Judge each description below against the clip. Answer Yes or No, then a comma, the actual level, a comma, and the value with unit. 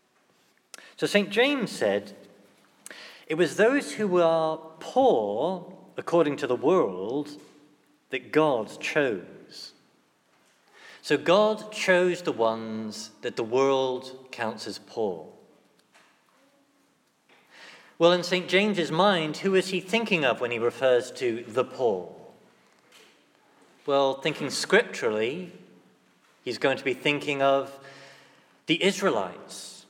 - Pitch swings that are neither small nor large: No, wide, 5.9 semitones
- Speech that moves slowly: Yes, slow, 110 wpm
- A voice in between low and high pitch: Yes, medium, 155 Hz